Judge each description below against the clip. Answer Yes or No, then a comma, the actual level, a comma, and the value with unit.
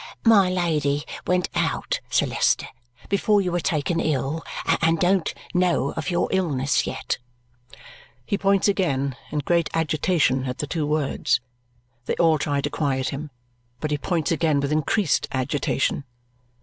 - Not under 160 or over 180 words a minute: No, average, 150 wpm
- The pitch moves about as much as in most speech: Yes, average, 4.1 semitones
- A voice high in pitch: No, medium, 155 Hz